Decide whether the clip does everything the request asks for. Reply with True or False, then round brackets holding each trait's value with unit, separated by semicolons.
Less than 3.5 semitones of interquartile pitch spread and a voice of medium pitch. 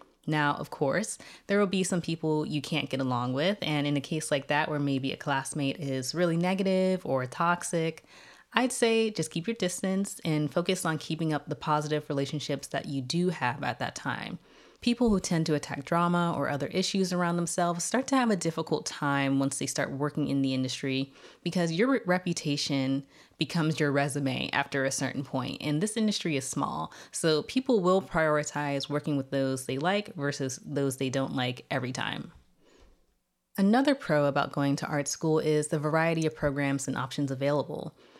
False (3.8 semitones; 150 Hz)